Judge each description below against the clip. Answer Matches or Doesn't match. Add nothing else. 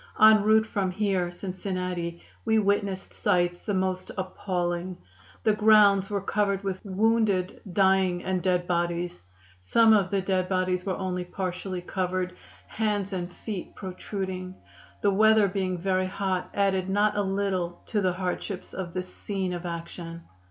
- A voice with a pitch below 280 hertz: Matches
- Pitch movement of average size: Doesn't match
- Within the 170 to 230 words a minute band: Doesn't match